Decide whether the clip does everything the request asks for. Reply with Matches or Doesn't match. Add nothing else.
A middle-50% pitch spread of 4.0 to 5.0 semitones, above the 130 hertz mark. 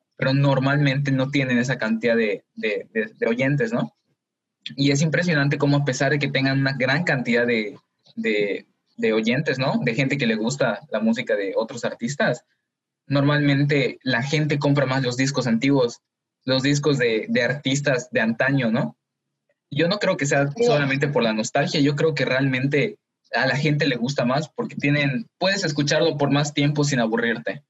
Doesn't match